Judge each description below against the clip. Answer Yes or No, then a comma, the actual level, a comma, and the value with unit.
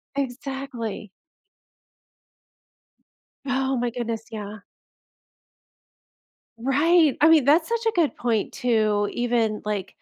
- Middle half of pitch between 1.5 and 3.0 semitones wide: No, average, 4.2 semitones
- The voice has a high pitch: Yes, high, 245 Hz